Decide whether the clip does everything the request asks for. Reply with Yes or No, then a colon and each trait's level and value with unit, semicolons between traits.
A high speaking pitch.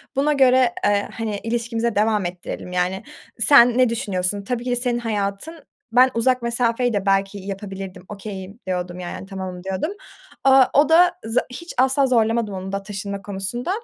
Yes: high, 220 Hz